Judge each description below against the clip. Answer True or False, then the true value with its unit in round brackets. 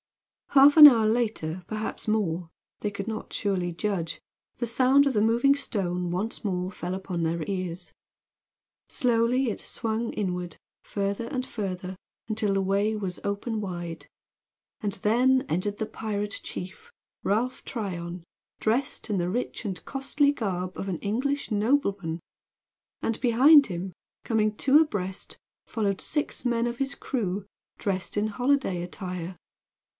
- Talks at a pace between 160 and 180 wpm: False (140 wpm)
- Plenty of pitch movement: False (4.5 semitones)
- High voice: True (210 Hz)